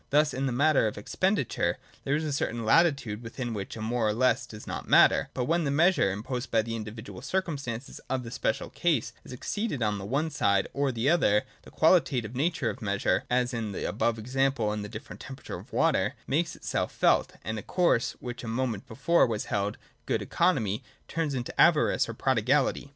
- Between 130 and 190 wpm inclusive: No, average, 200 wpm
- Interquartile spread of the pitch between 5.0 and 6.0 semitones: No, average, 4.6 semitones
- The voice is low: Yes, low, 125 Hz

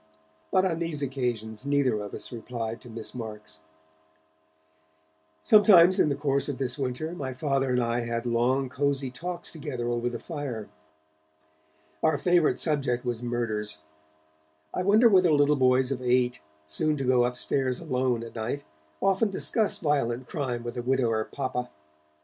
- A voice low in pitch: Yes, low, 130 Hz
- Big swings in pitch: No, average, 3.5 semitones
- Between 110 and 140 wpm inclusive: No, average, 155 wpm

